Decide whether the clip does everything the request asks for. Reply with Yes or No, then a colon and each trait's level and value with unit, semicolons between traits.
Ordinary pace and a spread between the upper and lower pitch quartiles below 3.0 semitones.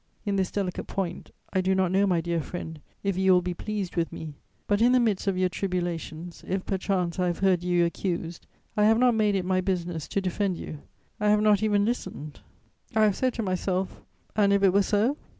No: fast, 220 wpm; narrow, 2.5 semitones